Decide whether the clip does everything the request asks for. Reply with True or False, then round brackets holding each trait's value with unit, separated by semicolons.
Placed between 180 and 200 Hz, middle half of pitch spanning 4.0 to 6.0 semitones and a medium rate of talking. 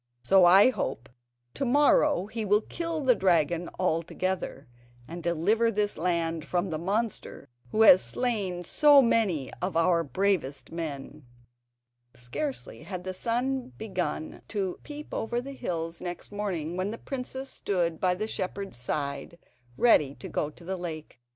True (185 Hz; 5.3 semitones; 150 wpm)